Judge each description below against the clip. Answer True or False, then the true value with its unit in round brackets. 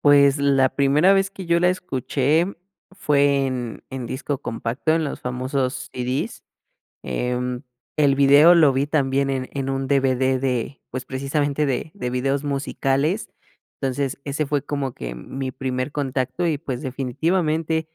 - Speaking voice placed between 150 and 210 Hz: False (135 Hz)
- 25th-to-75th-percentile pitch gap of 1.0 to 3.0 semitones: True (2.4 semitones)